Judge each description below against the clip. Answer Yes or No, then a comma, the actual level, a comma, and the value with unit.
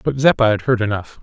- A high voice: No, low, 115 Hz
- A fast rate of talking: Yes, fast, 245 wpm